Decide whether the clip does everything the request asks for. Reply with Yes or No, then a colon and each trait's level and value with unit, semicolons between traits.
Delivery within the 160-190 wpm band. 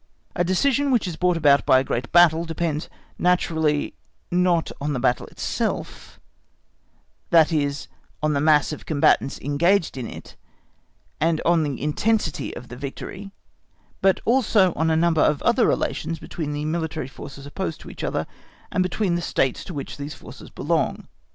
Yes: average, 165 wpm